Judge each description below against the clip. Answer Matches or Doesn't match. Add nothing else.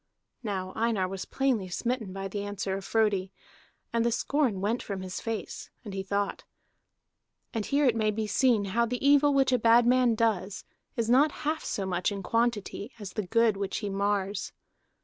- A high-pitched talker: Matches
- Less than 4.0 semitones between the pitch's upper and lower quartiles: Matches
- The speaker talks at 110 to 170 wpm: Doesn't match